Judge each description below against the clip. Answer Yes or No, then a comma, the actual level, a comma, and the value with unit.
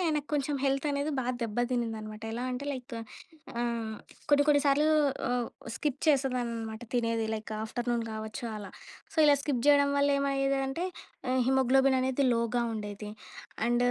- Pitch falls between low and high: No, very high, 250 Hz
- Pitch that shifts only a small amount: No, average, 3.3 semitones